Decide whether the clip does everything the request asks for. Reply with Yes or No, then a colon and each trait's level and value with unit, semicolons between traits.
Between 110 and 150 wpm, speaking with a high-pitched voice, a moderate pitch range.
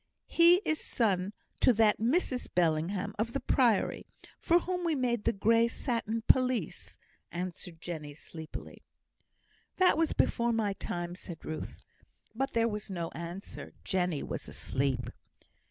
No: average, 140 wpm; high, 210 Hz; wide, 6.3 semitones